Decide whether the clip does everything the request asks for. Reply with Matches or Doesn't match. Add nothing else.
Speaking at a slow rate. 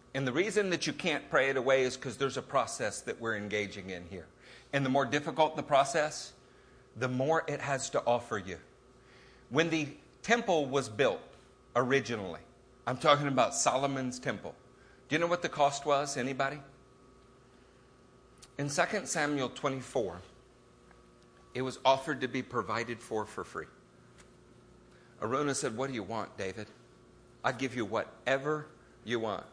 Doesn't match